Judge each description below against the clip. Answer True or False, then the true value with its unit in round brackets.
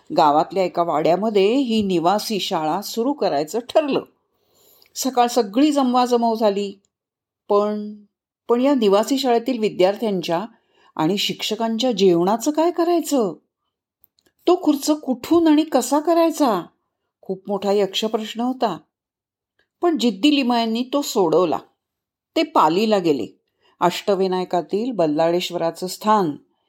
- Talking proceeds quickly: False (105 wpm)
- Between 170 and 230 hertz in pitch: True (225 Hz)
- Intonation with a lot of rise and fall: True (6.0 semitones)